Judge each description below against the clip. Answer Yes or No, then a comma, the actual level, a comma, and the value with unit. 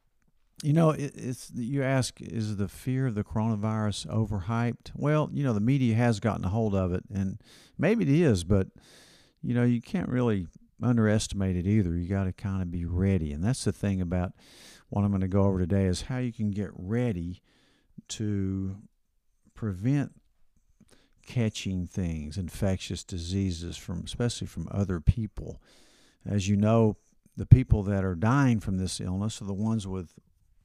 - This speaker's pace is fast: No, average, 170 wpm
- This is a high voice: No, low, 105 Hz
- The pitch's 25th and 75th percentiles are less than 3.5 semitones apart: No, average, 3.8 semitones